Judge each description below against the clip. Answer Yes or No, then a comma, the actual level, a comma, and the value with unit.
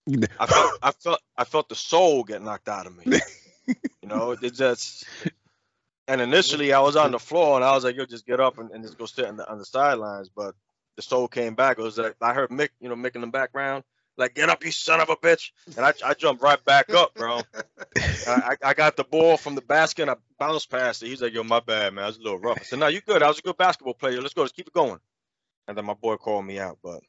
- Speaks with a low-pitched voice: Yes, low, 130 Hz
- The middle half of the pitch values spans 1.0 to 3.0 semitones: No, average, 4.3 semitones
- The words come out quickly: Yes, fast, 275 wpm